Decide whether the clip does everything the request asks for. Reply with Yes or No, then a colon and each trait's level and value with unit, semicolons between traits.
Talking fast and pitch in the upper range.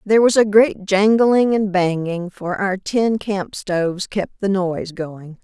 No: average, 175 wpm; high, 195 Hz